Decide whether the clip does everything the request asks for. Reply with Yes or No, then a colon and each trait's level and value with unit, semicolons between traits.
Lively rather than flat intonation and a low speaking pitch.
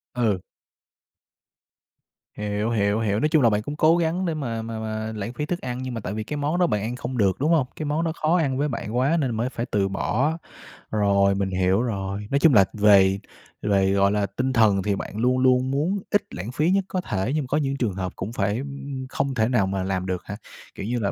Yes: wide, 5.7 semitones; low, 115 Hz